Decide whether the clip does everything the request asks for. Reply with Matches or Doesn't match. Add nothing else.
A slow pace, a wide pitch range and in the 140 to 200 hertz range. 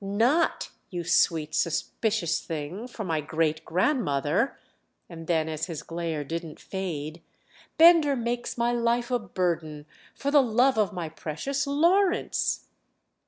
Matches